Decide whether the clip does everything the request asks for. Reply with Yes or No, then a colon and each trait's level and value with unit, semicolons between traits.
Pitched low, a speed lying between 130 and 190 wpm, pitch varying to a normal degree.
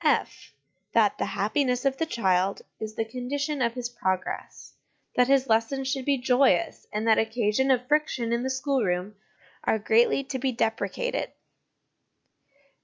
No: very high, 250 Hz; average, 150 wpm; average, 3.3 semitones